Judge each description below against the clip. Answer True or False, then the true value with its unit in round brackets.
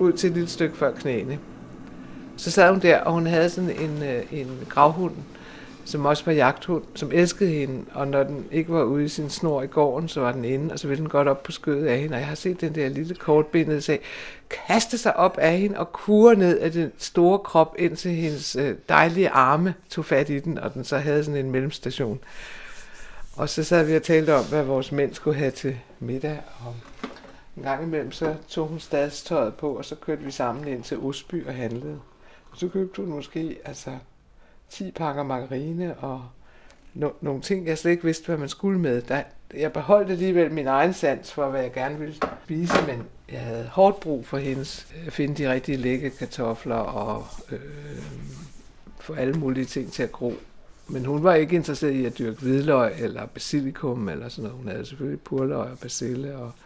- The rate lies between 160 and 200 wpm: False (210 wpm)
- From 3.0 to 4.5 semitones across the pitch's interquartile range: True (3.4 semitones)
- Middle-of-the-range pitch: True (150 Hz)